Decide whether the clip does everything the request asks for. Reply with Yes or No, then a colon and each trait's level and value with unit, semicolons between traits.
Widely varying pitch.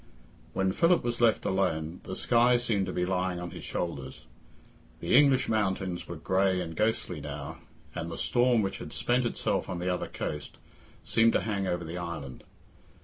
No: average, 4.8 semitones